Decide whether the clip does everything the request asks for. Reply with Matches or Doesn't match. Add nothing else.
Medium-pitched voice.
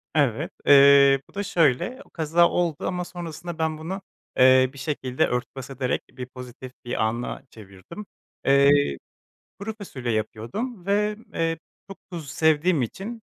Matches